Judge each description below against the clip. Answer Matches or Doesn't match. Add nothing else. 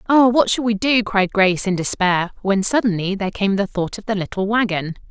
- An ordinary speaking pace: Doesn't match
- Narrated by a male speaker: Doesn't match